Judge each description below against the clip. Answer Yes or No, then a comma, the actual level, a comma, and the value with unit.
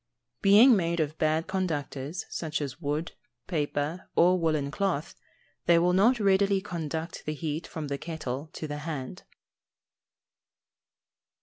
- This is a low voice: No, medium, 160 Hz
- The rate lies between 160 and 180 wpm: No, slow, 135 wpm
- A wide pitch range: No, average, 3.6 semitones